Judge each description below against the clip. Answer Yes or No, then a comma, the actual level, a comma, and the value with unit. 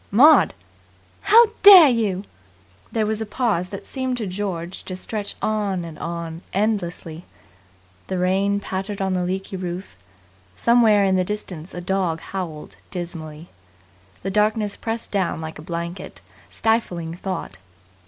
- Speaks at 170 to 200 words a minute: No, average, 140 wpm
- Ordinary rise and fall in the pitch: Yes, average, 3.5 semitones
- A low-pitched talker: No, high, 190 Hz